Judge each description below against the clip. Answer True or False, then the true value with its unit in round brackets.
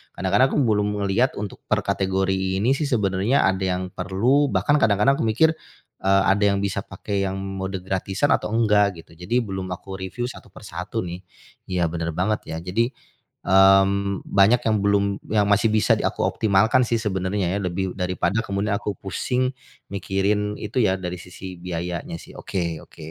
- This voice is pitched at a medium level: False (100 Hz)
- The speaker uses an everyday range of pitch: False (2.0 semitones)